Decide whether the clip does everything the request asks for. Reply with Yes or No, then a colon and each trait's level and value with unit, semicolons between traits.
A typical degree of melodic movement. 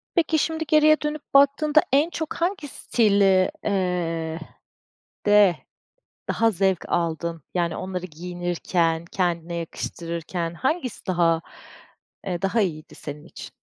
No: wide, 8.5 semitones